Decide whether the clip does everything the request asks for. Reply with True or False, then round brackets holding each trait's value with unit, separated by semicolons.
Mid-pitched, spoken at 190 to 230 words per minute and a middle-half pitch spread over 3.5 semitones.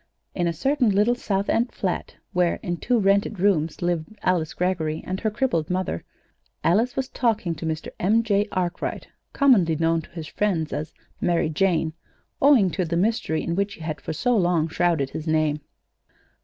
False (180 Hz; 180 wpm; 4.3 semitones)